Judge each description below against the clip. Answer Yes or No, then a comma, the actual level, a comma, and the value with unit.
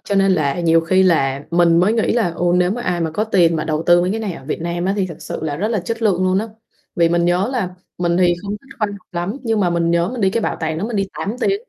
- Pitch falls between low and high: Yes, medium, 180 Hz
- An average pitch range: Yes, average, 3.4 semitones